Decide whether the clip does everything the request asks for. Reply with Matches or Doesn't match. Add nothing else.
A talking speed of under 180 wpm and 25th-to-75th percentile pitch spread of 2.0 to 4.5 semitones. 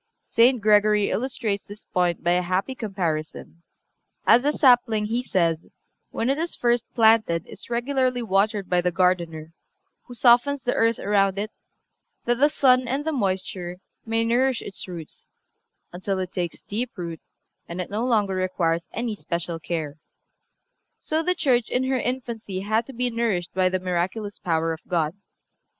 Doesn't match